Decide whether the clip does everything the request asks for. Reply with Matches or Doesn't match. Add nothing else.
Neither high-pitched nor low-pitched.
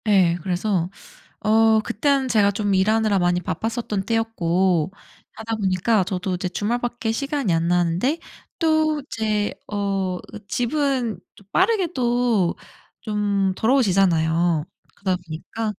Doesn't match